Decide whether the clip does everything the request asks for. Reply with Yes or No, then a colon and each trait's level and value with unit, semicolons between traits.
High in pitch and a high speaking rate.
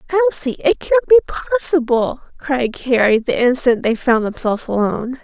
No: very high, 270 Hz; average, 150 wpm